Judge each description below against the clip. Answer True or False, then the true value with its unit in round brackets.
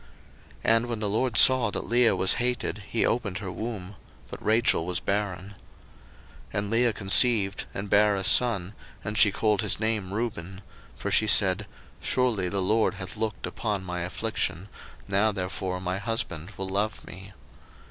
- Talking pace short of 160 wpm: False (170 wpm)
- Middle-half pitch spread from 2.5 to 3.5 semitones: True (2.9 semitones)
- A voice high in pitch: False (100 Hz)